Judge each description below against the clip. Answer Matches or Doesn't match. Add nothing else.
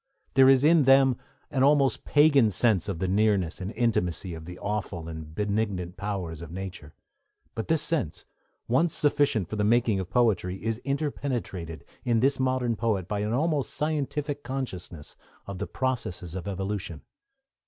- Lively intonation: Matches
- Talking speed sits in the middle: Matches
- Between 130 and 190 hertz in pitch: Doesn't match